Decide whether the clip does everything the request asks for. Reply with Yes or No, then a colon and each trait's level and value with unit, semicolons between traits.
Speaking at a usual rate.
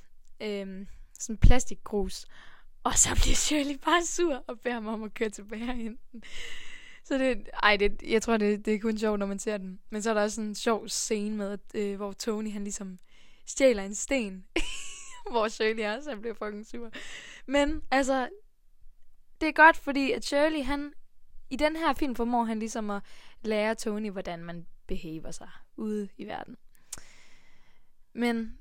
Yes: average, 180 wpm